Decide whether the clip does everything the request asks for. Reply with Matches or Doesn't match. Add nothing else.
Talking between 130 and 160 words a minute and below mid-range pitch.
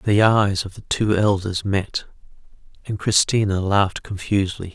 Matches